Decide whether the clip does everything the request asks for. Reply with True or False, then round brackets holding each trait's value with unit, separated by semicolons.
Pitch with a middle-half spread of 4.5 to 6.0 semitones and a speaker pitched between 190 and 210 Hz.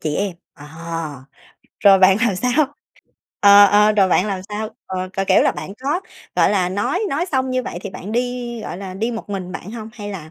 False (4.1 semitones; 205 Hz)